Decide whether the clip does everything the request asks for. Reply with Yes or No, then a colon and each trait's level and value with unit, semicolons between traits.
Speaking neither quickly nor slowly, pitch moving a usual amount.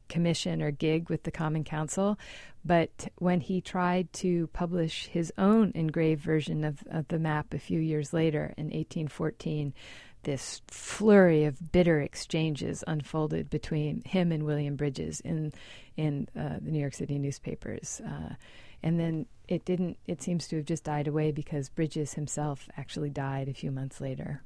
No: average, 165 wpm; narrow, 2.2 semitones